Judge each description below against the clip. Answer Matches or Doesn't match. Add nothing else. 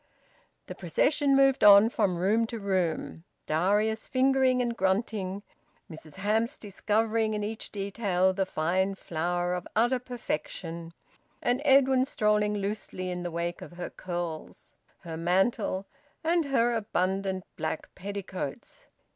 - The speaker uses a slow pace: Matches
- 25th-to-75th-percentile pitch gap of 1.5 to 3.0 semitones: Doesn't match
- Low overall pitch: Doesn't match